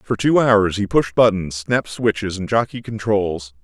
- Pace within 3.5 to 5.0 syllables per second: Yes, 4.5 syllables/s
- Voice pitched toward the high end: No, low, 105 Hz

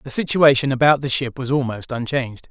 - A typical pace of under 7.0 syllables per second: Yes, 5.8 syllables/s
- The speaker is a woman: No, male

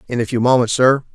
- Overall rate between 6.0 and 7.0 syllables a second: Yes, 6.6 syllables/s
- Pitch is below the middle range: Yes, low, 125 Hz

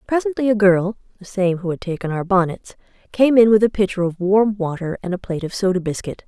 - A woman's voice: Yes, female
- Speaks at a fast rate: Yes, fast, 230 wpm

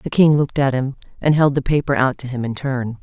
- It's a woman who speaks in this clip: Yes, female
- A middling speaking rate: No, fast, 280 wpm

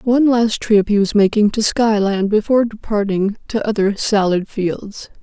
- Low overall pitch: No, high, 210 Hz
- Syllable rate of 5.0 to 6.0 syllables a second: No, 4.7 syllables/s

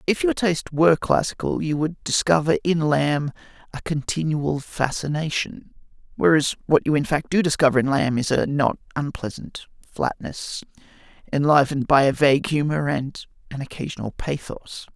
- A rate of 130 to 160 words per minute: Yes, average, 145 wpm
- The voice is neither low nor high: Yes, medium, 150 Hz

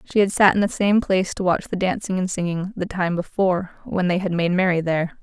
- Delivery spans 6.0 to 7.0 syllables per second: Yes, 6.1 syllables/s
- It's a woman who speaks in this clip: Yes, female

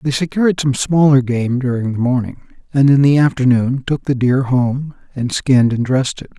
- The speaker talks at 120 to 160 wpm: No, average, 195 wpm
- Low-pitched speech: Yes, low, 130 Hz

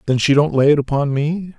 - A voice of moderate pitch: Yes, medium, 145 Hz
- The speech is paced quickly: Yes, fast, 265 wpm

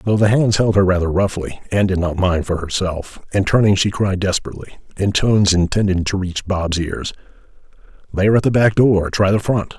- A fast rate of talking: Yes, fast, 210 wpm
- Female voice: No, male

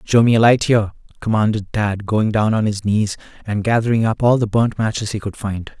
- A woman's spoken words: No, male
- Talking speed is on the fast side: Yes, fast, 230 wpm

